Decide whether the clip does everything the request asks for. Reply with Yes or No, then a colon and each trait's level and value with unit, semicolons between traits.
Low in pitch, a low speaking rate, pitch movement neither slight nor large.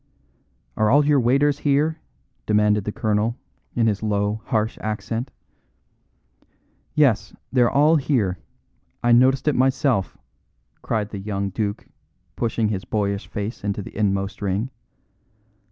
Yes: low, 110 Hz; slow, 125 wpm; average, 4.2 semitones